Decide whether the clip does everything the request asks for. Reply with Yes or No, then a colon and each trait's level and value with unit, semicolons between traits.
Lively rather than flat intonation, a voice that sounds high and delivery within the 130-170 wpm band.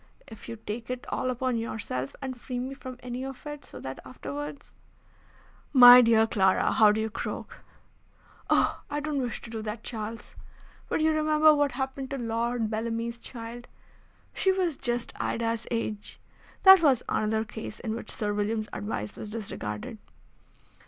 No: average, 3.1 semitones; high, 230 Hz; average, 165 wpm